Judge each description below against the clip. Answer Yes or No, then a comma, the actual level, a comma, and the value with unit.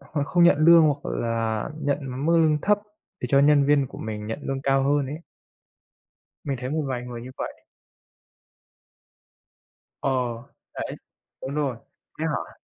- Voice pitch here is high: No, medium, 140 Hz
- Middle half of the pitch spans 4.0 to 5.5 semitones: No, average, 2.8 semitones